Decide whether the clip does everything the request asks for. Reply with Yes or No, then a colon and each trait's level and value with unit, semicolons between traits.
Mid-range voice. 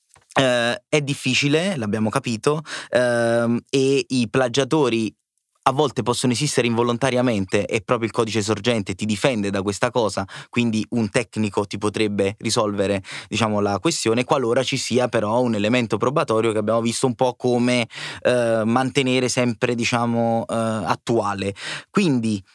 No: low, 120 Hz